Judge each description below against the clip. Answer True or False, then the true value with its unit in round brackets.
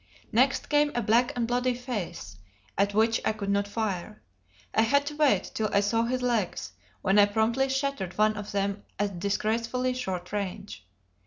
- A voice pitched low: False (220 Hz)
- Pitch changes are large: False (3.7 semitones)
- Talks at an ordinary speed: True (175 wpm)